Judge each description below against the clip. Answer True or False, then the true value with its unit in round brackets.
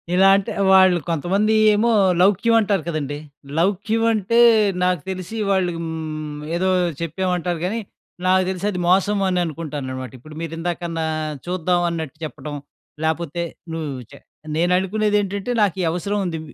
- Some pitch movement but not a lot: True (3.2 semitones)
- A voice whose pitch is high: False (180 Hz)